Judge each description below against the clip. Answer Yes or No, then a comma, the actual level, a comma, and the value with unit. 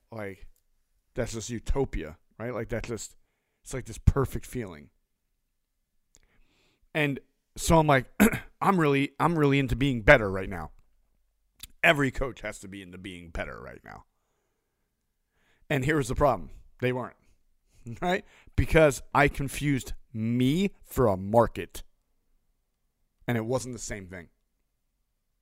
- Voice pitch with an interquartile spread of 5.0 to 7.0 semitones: Yes, wide, 5.4 semitones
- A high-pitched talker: No, low, 125 Hz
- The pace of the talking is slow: Yes, slow, 130 wpm